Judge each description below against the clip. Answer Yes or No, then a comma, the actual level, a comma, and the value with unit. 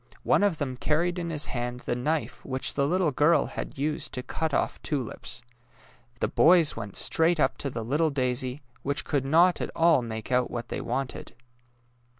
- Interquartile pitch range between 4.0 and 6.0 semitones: Yes, average, 4.4 semitones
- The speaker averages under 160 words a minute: No, average, 185 wpm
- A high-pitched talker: No, medium, 140 Hz